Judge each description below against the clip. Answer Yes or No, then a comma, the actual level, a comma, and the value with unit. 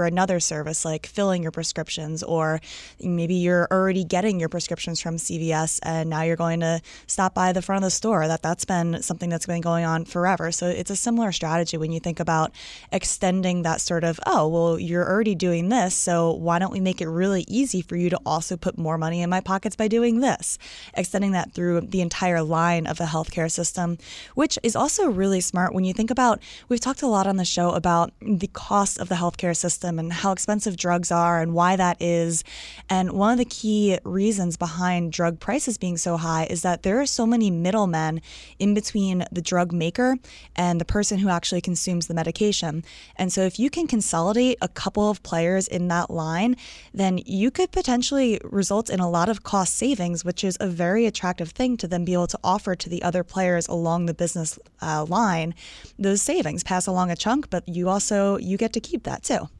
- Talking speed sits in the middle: No, fast, 210 wpm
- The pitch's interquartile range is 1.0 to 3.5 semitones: Yes, average, 2.9 semitones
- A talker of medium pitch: Yes, medium, 180 Hz